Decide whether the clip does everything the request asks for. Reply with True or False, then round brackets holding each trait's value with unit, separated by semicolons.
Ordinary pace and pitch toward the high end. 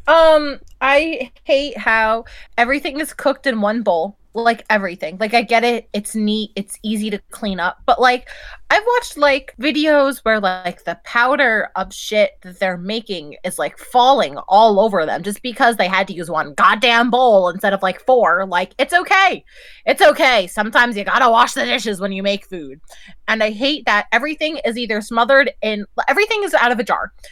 True (195 wpm; 230 Hz)